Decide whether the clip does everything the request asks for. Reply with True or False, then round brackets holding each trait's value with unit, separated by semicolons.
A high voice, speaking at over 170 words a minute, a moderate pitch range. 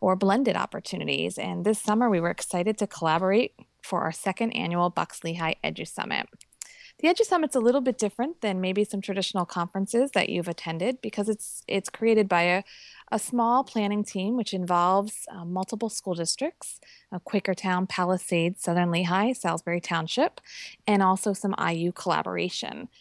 False (195 Hz; 160 wpm; 4.1 semitones)